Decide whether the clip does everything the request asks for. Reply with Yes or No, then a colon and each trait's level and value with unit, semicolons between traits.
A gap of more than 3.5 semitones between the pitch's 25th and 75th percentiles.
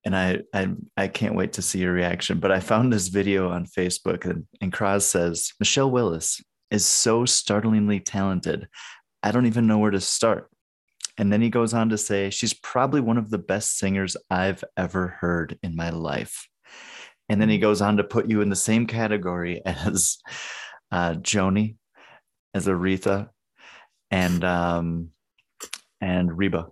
No: average, 3.1 semitones